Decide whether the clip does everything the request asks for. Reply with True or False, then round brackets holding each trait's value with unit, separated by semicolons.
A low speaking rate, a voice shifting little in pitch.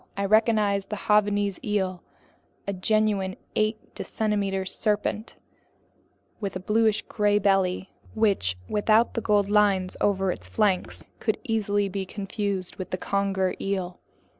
True (130 wpm; 1.8 semitones)